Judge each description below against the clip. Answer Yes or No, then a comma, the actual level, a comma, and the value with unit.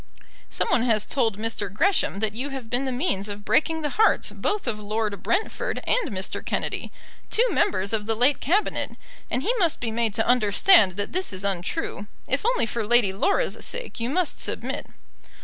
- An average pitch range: No, wide, 7.7 semitones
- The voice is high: Yes, high, 235 Hz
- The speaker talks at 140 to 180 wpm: No, average, 190 wpm